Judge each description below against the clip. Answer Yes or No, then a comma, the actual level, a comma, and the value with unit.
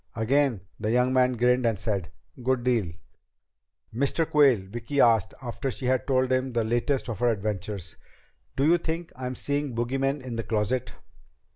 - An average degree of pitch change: Yes, average, 3.0 semitones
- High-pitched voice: No, low, 125 Hz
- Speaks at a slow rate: No, average, 160 wpm